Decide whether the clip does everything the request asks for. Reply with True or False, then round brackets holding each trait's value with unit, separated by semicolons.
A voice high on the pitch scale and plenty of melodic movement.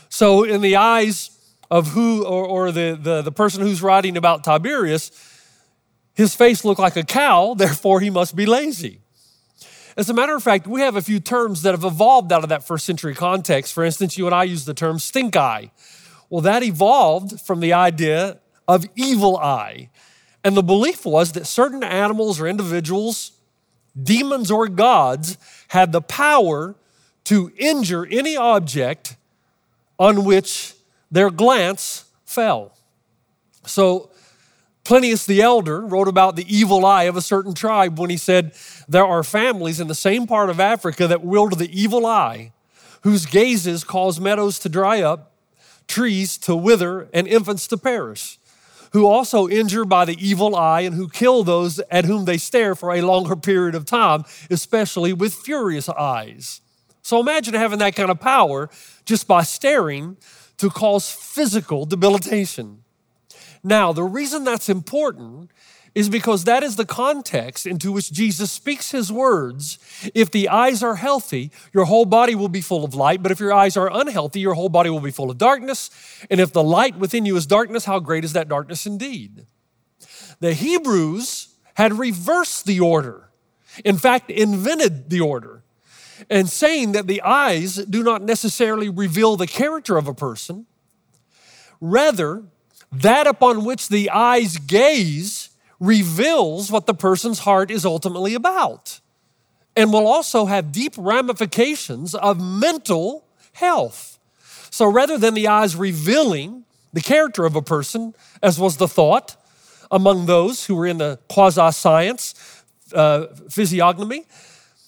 False (195 Hz; 4.6 semitones)